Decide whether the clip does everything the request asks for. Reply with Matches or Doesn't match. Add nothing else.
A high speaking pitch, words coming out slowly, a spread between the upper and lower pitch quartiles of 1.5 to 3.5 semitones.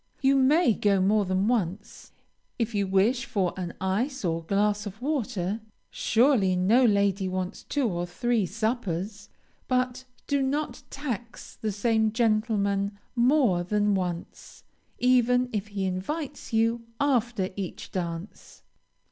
Doesn't match